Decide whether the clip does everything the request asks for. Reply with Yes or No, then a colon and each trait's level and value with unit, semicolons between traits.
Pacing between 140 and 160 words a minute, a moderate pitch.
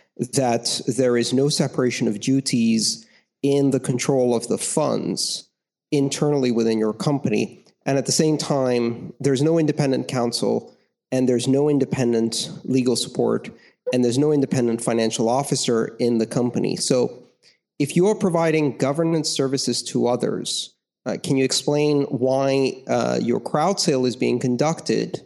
No: average, 145 wpm; low, 130 Hz